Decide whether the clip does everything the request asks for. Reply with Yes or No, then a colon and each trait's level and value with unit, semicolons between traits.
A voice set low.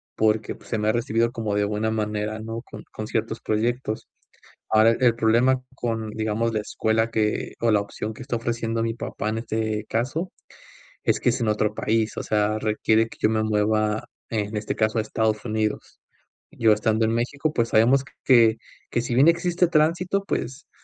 Yes: low, 110 Hz